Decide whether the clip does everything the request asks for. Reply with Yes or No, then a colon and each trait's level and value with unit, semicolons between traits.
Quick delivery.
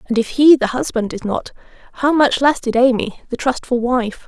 Yes: fast, 210 wpm